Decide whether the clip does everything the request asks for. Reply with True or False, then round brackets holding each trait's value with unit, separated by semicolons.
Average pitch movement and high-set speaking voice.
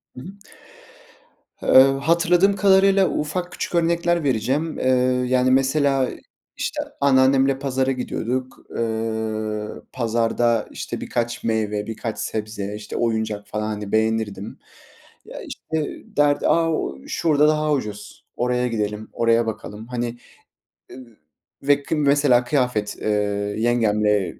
False (4.6 semitones; 125 Hz)